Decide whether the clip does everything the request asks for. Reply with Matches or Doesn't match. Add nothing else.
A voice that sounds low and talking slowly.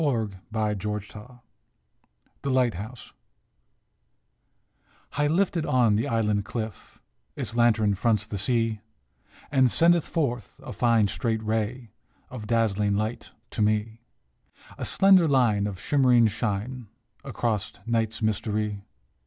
Matches